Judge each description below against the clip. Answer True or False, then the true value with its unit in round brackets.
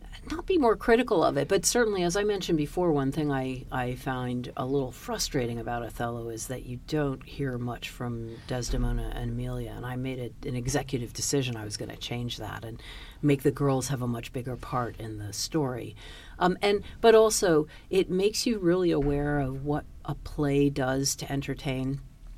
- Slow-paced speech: False (195 wpm)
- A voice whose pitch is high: False (135 Hz)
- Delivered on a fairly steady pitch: False (3.8 semitones)